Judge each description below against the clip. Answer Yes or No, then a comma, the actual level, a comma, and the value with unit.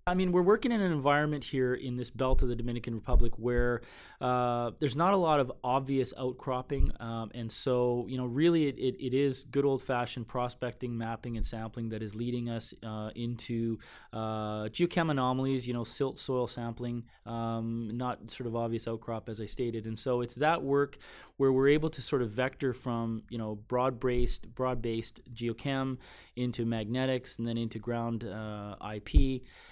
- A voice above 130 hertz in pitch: No, low, 120 Hz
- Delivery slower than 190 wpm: Yes, average, 180 wpm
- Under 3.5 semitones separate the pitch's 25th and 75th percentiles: Yes, narrow, 2.4 semitones